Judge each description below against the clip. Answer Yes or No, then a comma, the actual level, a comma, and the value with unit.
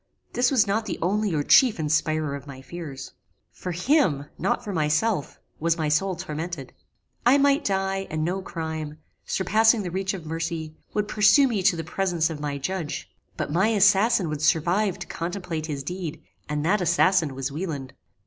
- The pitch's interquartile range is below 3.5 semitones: No, average, 4.2 semitones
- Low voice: No, medium, 175 Hz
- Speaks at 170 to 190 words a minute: Yes, average, 175 wpm